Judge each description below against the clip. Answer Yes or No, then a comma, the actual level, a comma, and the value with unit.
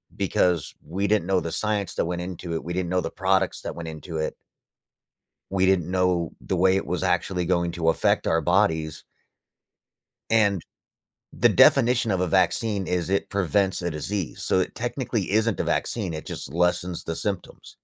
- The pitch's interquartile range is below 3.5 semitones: Yes, narrow, 2.6 semitones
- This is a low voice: Yes, very low, 90 Hz